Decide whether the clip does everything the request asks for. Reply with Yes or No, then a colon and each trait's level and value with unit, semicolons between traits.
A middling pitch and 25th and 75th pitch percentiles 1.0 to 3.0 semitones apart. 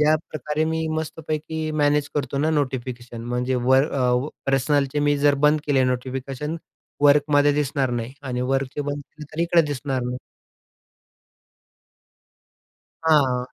Yes: medium, 145 Hz; narrow, 2.6 semitones